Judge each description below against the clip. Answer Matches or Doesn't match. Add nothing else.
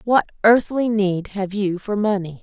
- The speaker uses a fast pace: Doesn't match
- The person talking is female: Matches